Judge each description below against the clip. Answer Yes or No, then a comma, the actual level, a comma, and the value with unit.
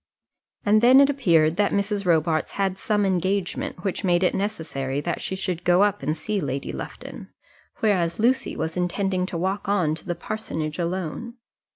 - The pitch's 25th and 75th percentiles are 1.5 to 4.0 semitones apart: Yes, average, 3.5 semitones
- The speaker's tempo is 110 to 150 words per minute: No, average, 175 wpm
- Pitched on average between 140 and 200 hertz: Yes, medium, 185 Hz